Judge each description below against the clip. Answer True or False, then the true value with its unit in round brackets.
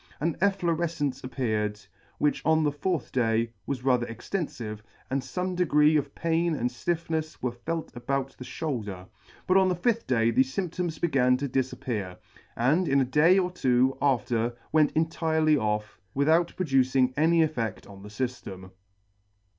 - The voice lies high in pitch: False (140 Hz)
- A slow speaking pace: False (155 wpm)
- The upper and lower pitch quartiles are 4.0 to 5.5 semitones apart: True (5.0 semitones)